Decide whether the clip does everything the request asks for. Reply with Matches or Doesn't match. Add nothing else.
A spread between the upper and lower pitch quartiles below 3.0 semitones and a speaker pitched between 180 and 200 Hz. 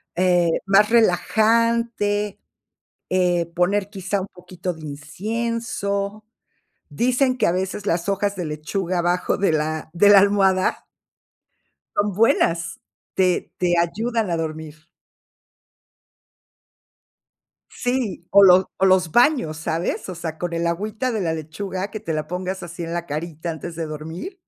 Doesn't match